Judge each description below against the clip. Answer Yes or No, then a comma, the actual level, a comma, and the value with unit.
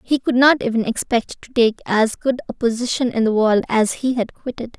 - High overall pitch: Yes, high, 235 Hz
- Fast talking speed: Yes, fast, 225 wpm